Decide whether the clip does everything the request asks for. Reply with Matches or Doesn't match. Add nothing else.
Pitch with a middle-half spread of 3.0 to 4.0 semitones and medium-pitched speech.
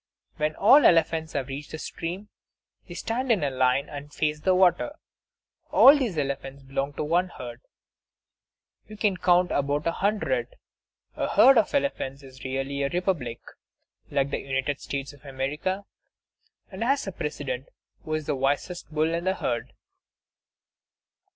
Doesn't match